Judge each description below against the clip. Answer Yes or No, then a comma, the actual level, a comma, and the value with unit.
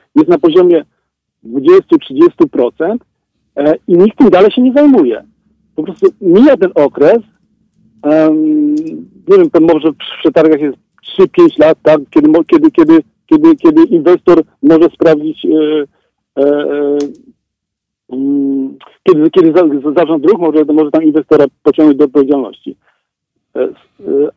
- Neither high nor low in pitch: Yes, medium, 180 Hz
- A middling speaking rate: No, slow, 105 wpm